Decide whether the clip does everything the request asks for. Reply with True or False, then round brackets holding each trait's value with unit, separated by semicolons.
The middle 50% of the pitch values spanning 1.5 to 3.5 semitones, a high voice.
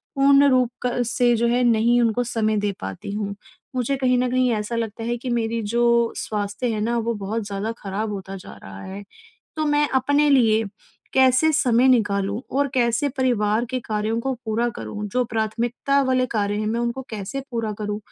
True (3.0 semitones; 235 Hz)